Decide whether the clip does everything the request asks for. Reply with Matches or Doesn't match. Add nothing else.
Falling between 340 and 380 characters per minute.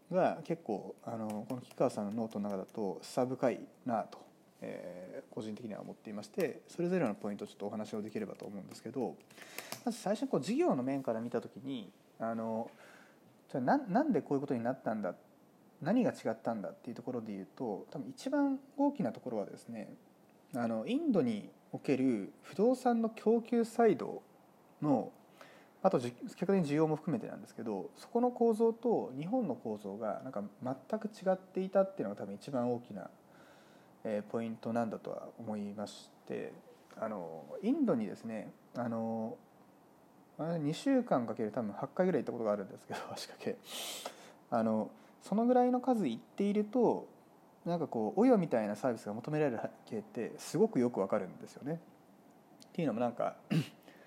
Matches